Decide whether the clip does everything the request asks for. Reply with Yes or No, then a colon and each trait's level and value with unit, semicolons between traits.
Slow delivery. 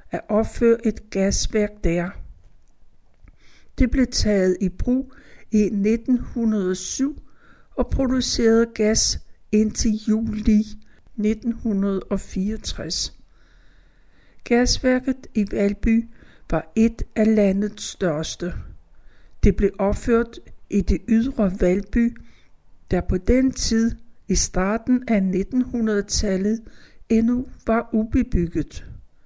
Yes: slow, 90 wpm